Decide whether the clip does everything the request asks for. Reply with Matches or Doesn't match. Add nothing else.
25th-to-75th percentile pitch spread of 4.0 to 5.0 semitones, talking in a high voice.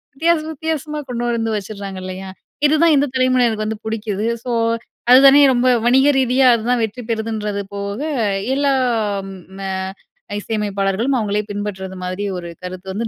Matches